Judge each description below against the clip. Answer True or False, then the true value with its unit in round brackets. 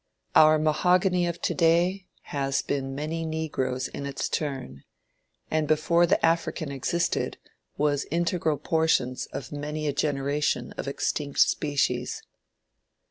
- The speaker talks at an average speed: False (125 wpm)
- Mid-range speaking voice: True (150 Hz)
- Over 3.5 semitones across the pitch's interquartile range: False (2.8 semitones)